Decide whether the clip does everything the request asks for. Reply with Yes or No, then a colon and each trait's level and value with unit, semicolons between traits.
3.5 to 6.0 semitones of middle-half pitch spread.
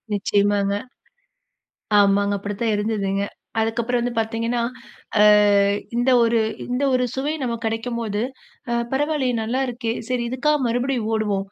No: average, 3.1 semitones